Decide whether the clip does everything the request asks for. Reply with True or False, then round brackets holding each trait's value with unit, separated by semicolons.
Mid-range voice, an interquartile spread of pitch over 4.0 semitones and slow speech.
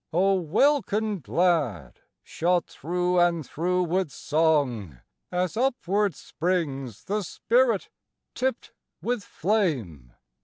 True (180 Hz; 5.1 semitones; 100 wpm)